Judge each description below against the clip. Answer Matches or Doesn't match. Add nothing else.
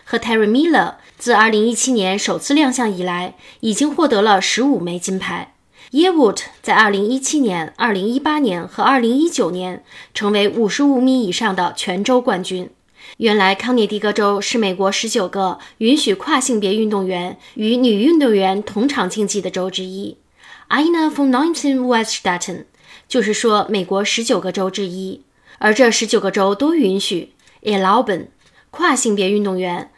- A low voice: Doesn't match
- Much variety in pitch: Doesn't match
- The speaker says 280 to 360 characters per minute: Doesn't match